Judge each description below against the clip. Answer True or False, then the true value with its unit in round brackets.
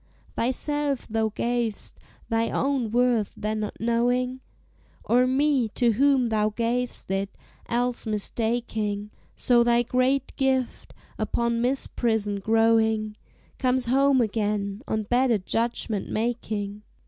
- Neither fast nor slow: False (110 wpm)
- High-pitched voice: True (235 Hz)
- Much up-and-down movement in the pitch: False (2.6 semitones)